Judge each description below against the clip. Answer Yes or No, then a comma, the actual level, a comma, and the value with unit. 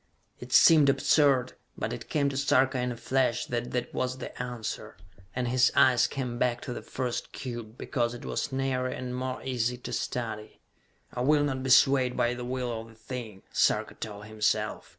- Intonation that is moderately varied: No, narrow, 1.8 semitones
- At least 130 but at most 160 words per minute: No, average, 190 wpm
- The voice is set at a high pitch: No, low, 125 Hz